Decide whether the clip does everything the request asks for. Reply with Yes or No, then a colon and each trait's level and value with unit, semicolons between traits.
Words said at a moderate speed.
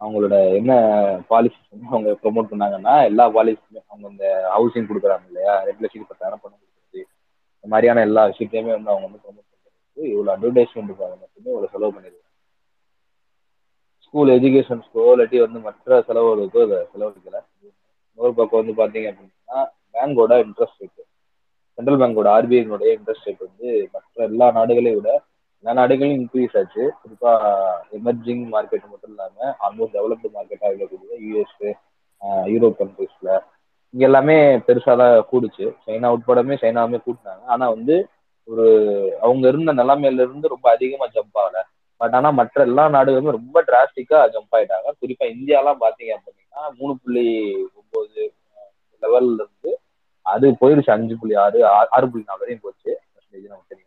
No: fast, 135 wpm